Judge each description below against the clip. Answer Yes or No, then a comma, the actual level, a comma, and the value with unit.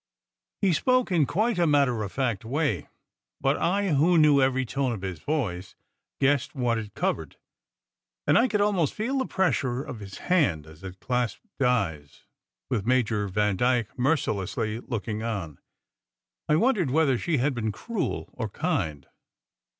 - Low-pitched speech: Yes, low, 130 Hz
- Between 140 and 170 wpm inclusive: Yes, average, 160 wpm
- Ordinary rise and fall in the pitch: No, wide, 7.0 semitones